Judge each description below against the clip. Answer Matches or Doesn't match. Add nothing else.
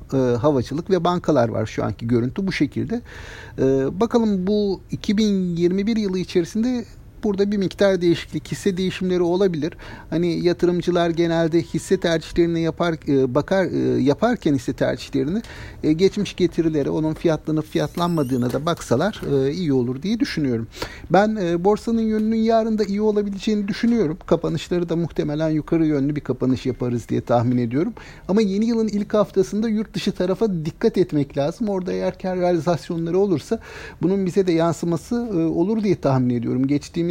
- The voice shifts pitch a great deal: Doesn't match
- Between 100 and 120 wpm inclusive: Doesn't match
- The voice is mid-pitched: Matches